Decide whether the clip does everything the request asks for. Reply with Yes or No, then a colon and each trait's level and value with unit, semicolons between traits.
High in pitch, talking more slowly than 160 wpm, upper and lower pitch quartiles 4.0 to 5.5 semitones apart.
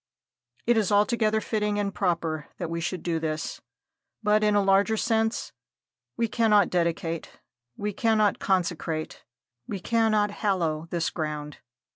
Yes: high, 200 Hz; slow, 135 wpm; average, 4.3 semitones